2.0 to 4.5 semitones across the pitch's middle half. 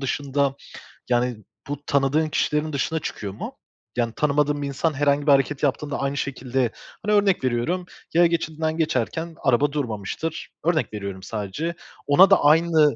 Yes: average, 3.5 semitones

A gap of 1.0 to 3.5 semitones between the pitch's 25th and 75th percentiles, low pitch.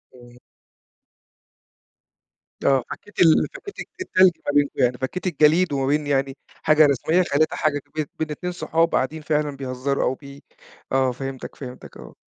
No: average, 2.9 semitones; medium, 145 Hz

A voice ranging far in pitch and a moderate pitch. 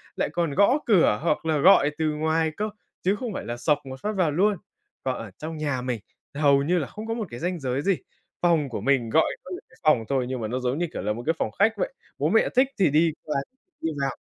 Yes: wide, 5.7 semitones; medium, 155 Hz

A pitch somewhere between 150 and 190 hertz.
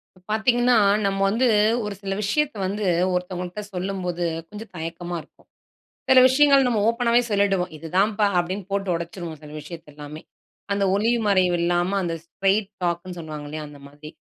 Yes: medium, 185 Hz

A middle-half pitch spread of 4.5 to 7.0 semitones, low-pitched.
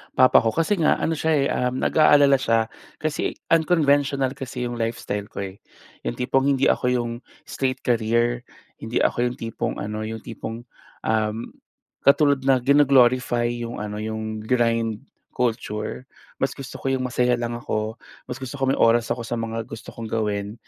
No: average, 3.0 semitones; low, 120 Hz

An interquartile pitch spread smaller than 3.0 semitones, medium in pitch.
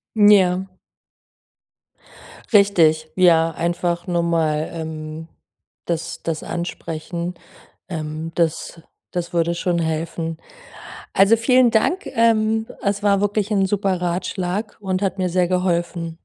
No: average, 3.3 semitones; medium, 175 Hz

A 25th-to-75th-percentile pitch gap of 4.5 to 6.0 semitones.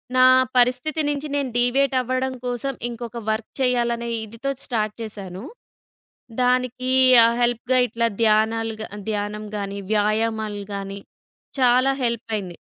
No: average, 2.9 semitones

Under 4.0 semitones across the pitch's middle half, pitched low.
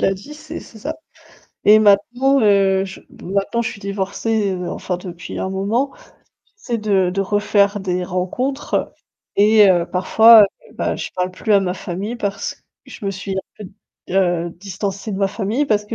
No: narrow, 2.5 semitones; high, 200 Hz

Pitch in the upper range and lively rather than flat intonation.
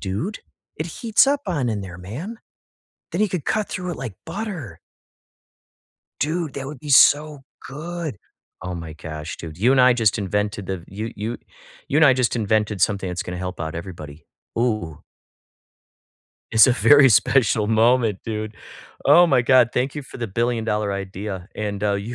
No: low, 115 Hz; wide, 6.4 semitones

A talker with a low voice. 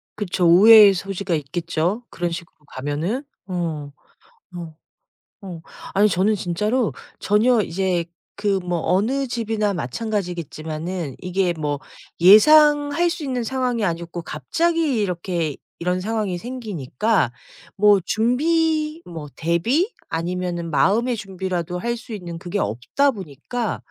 No: high, 190 Hz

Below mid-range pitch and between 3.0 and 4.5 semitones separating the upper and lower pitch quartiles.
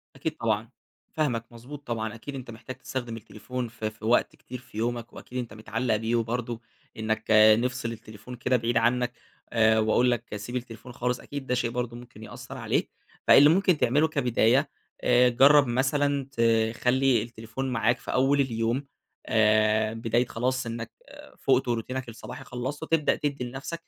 No: low, 120 Hz; narrow, 2.5 semitones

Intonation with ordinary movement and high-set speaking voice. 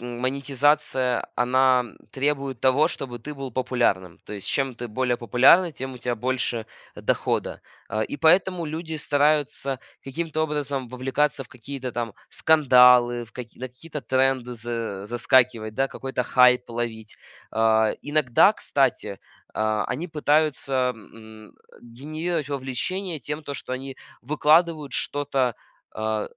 No: average, 3.4 semitones; low, 130 Hz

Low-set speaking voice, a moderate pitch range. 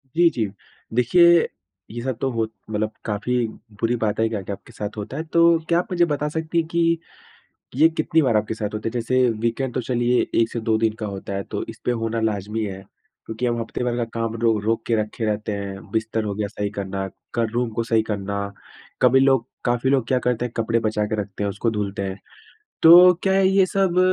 Yes: low, 115 Hz; average, 3.6 semitones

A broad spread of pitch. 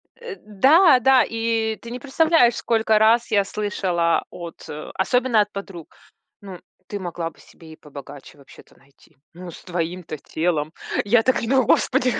Yes: wide, 5.9 semitones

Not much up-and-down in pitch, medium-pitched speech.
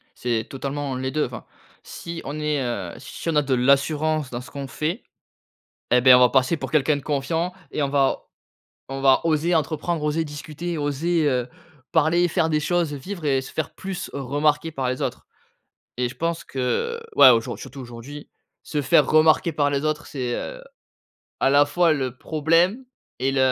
No: average, 3.3 semitones; medium, 145 Hz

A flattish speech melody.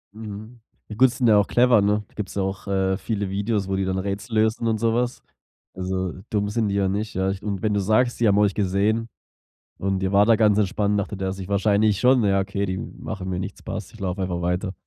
Yes: narrow, 2.2 semitones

